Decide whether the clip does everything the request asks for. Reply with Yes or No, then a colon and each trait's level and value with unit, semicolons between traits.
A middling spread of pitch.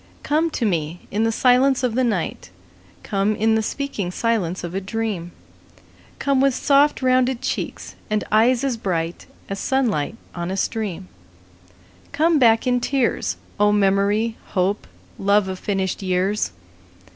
Yes: average, 4.7 semitones